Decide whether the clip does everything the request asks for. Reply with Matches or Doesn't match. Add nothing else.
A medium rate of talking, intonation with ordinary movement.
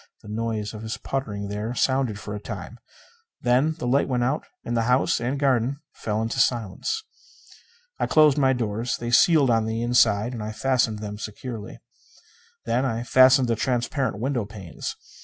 Matches